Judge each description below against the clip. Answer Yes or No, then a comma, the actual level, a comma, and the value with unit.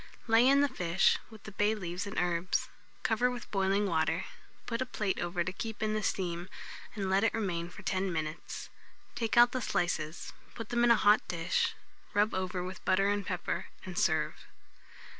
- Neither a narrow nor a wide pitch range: Yes, average, 3.9 semitones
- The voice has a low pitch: No, high, 195 Hz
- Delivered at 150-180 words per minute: No, average, 190 wpm